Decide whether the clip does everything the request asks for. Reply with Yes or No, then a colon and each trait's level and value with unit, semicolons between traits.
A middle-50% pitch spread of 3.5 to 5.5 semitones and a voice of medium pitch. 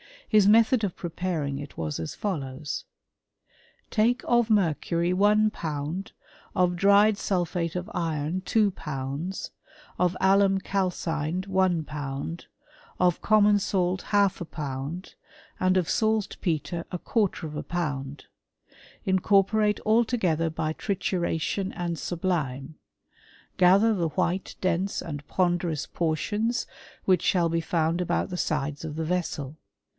Yes: average, 3.9 semitones; medium, 175 Hz